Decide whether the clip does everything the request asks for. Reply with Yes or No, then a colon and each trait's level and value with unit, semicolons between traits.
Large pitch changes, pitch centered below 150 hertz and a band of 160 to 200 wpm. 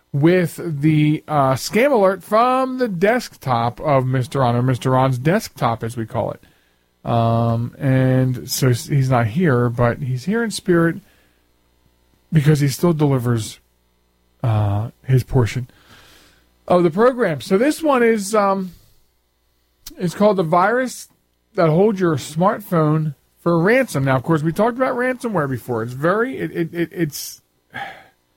No: wide, 7.6 semitones; medium, 140 Hz; average, 140 wpm